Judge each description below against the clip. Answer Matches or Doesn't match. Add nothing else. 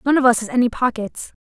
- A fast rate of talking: Matches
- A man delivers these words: Doesn't match